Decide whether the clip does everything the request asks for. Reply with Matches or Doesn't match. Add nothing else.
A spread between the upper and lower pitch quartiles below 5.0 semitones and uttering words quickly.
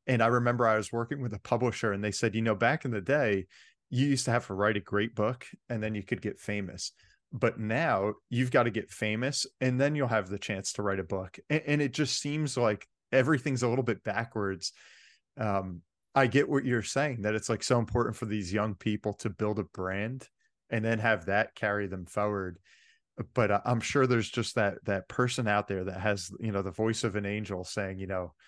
Matches